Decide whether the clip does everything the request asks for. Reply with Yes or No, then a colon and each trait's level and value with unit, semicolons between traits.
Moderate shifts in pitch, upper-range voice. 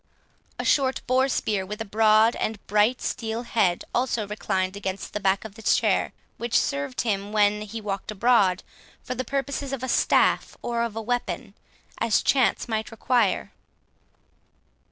Yes: average, 3.1 semitones; high, 220 Hz